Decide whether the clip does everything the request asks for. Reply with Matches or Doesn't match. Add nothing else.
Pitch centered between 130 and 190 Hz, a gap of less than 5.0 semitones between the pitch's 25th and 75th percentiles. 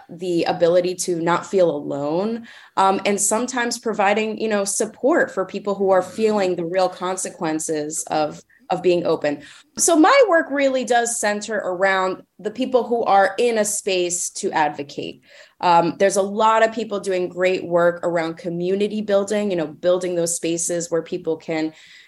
Matches